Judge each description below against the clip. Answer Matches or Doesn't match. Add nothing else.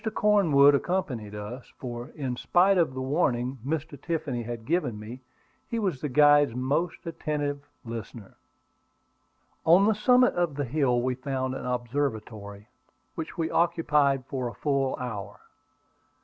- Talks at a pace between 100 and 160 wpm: Matches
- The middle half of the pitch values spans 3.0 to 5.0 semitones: Matches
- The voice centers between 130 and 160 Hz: Matches